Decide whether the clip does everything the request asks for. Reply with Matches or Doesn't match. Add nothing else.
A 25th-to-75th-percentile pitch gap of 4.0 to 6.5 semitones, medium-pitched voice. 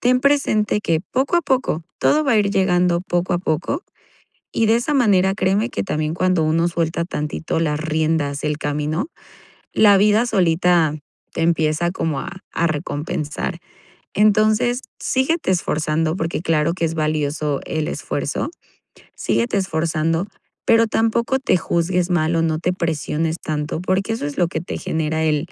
Matches